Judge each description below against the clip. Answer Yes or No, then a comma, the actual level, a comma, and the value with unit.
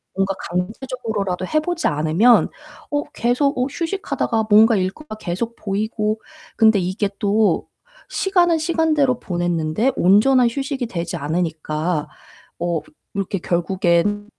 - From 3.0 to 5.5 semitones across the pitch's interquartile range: No, wide, 6.2 semitones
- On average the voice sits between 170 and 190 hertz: No, high, 210 Hz